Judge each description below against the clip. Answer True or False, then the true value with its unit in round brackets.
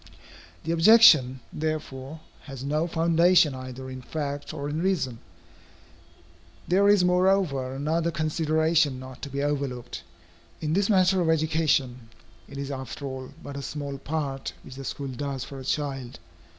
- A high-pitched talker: False (145 Hz)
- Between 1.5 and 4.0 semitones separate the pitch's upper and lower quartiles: True (3.5 semitones)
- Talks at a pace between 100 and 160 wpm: True (150 wpm)